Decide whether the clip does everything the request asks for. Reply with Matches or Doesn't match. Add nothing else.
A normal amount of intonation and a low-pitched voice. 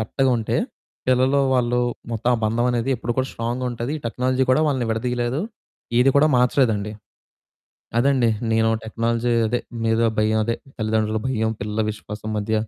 Doesn't match